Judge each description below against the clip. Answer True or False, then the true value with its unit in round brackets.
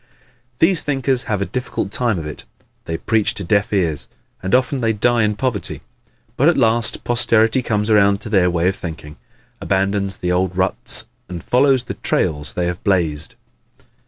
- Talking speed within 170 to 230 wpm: True (175 wpm)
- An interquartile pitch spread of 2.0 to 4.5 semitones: False (5.0 semitones)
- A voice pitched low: True (100 Hz)